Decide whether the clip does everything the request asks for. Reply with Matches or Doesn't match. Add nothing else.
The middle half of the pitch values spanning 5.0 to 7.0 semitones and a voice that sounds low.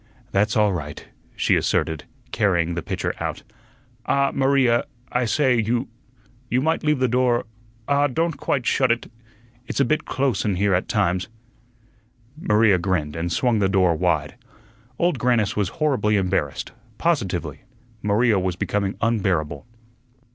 Matches